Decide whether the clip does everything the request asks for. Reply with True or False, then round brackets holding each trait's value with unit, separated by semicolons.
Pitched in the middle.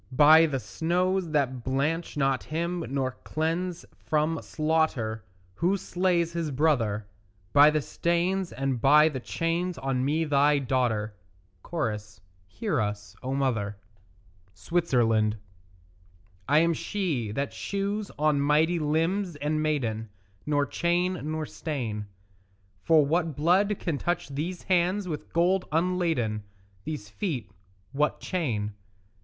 True (155 Hz)